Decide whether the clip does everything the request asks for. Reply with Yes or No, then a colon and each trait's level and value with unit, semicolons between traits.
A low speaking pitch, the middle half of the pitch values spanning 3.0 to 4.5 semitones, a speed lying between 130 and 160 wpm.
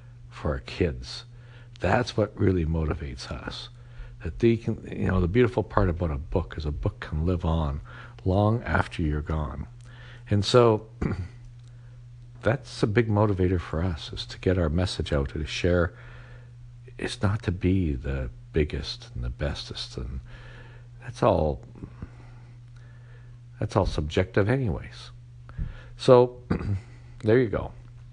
No: low, 110 Hz; wide, 5.4 semitones; average, 140 wpm